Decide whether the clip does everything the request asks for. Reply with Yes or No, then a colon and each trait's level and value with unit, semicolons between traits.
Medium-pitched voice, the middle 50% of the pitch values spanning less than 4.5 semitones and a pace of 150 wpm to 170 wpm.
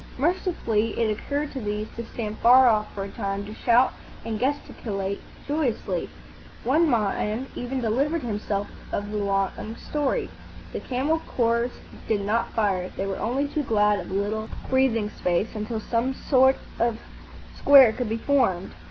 No: high, 230 Hz; average, 4.0 semitones; average, 160 wpm